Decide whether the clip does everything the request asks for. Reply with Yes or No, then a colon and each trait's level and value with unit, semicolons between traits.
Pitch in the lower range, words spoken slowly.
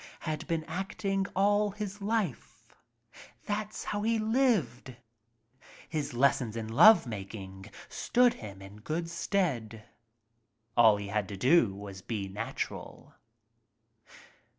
No: medium, 150 Hz; slow, 120 wpm